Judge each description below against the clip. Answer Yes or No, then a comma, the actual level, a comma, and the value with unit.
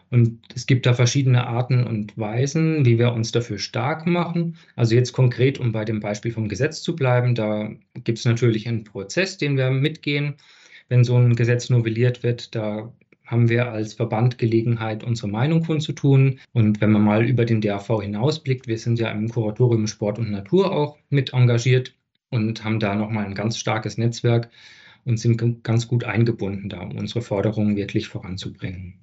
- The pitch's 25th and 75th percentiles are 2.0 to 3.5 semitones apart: Yes, average, 2.8 semitones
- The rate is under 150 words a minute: No, average, 180 wpm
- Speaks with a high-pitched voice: No, low, 120 Hz